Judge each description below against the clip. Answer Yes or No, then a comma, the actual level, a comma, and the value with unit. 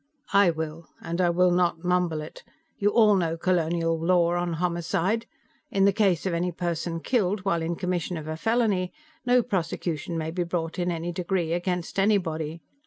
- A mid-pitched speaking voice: Yes, medium, 175 Hz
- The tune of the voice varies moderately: No, narrow, 2.1 semitones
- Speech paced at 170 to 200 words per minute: Yes, average, 175 wpm